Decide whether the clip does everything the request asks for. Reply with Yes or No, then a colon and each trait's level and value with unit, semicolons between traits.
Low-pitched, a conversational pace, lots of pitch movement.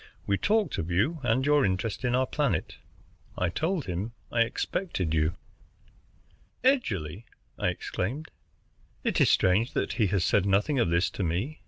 Yes: low, 110 Hz; average, 160 wpm; wide, 7.7 semitones